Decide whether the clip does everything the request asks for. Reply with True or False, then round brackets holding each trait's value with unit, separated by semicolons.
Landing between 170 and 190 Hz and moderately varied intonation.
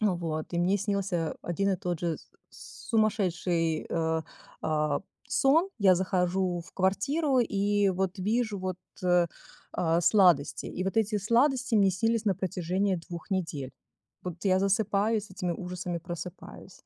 True (185 Hz; 3.0 semitones)